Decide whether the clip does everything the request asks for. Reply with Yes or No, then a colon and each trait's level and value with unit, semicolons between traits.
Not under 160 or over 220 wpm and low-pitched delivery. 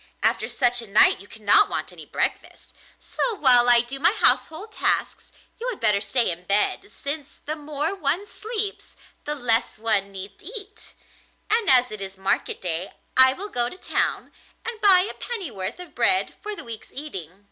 No: average, 180 wpm; very high, 270 Hz